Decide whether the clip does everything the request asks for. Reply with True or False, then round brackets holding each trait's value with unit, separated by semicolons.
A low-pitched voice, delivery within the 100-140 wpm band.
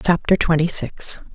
False (170 Hz; 135 wpm)